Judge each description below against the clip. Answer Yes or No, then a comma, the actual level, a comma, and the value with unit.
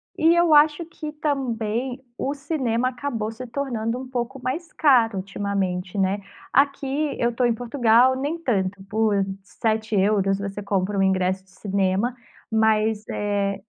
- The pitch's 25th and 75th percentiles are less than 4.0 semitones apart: No, average, 4.9 semitones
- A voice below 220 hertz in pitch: No, high, 225 Hz